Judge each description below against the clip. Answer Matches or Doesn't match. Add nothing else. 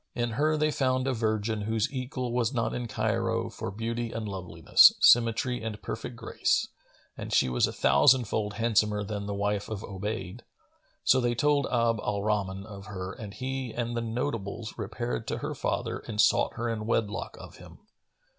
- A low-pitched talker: Matches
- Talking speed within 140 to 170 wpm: Doesn't match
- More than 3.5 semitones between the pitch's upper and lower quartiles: Doesn't match